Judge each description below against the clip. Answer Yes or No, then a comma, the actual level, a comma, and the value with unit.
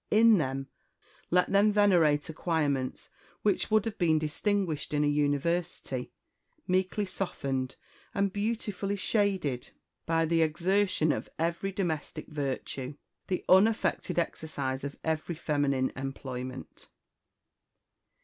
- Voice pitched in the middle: Yes, medium, 160 Hz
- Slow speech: Yes, slow, 110 wpm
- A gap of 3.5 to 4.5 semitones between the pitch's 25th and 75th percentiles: No, wide, 5.4 semitones